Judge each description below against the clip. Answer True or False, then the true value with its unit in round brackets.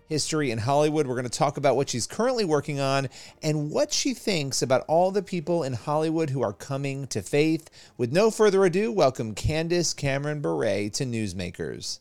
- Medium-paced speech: True (190 wpm)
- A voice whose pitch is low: False (150 Hz)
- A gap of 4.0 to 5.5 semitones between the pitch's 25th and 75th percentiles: True (4.6 semitones)